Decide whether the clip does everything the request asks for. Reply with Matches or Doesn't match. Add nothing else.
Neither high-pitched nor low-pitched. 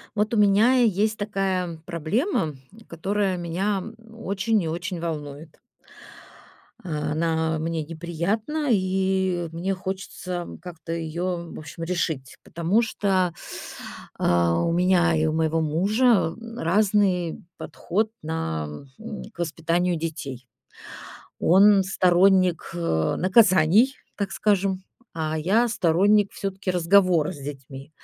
Matches